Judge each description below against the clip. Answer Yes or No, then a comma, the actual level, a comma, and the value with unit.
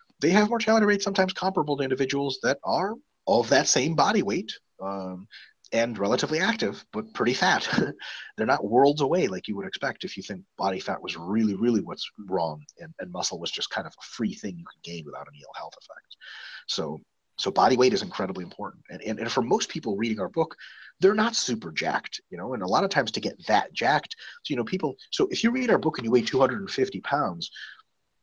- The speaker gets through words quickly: Yes, fast, 220 wpm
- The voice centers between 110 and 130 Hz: No, medium, 140 Hz